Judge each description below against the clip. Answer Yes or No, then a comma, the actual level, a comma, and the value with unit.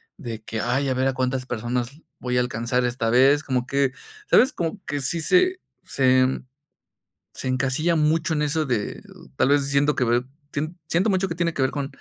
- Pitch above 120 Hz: Yes, low, 135 Hz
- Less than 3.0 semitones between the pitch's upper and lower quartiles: No, average, 3.8 semitones